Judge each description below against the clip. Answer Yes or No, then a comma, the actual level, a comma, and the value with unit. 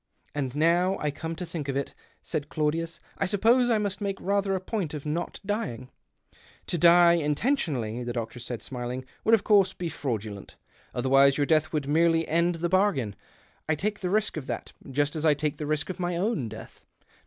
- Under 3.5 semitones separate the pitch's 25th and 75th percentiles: No, average, 5.2 semitones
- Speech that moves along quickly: Yes, fast, 220 wpm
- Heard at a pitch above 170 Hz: No, medium, 160 Hz